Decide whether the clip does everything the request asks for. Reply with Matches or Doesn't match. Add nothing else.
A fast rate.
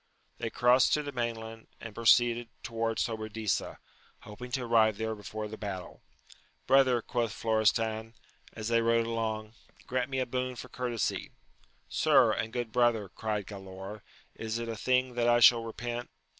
Doesn't match